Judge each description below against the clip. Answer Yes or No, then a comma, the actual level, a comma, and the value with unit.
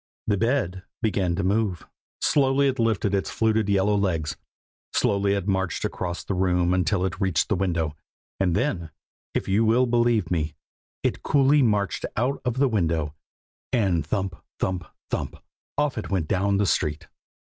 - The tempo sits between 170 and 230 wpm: No, average, 160 wpm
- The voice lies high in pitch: No, low, 100 Hz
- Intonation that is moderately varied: Yes, average, 4.0 semitones